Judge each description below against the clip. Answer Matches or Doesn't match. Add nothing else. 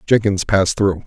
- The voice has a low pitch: Matches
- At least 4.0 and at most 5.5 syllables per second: Matches